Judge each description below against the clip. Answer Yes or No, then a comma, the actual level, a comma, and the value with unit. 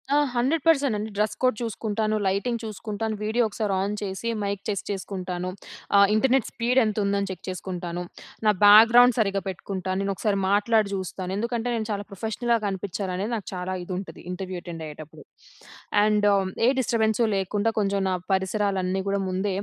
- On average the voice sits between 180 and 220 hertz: Yes, high, 205 Hz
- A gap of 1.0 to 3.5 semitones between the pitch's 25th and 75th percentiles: Yes, average, 2.7 semitones